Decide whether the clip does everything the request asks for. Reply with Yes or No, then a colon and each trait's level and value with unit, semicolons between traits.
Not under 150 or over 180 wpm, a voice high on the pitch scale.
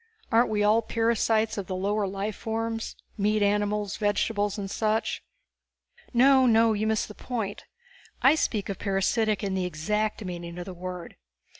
Yes: average, 160 wpm; high, 210 Hz